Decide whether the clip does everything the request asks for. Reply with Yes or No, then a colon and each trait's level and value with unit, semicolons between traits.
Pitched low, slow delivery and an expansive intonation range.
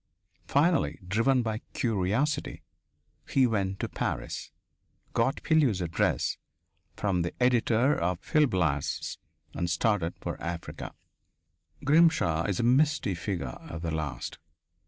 Yes: low, 105 Hz; slow, 115 wpm; wide, 7.4 semitones